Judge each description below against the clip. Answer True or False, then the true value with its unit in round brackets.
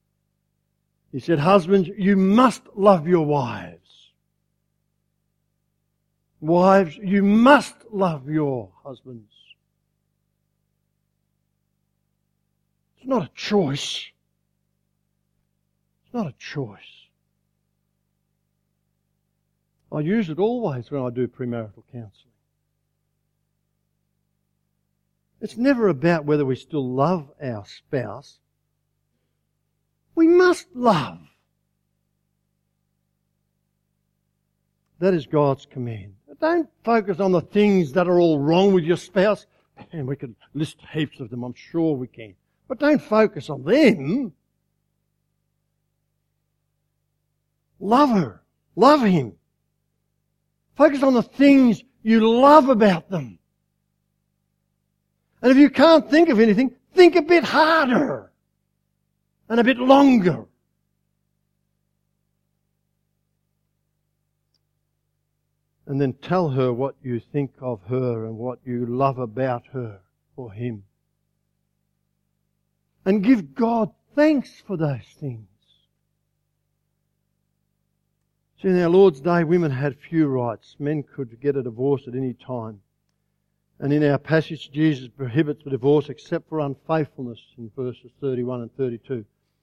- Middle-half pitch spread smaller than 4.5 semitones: False (5.6 semitones)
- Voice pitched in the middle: True (150 Hz)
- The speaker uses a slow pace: True (105 wpm)